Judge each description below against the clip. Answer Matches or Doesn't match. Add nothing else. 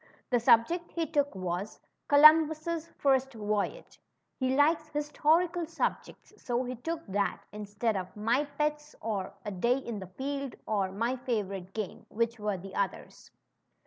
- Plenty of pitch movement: Matches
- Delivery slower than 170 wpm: Matches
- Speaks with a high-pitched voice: Matches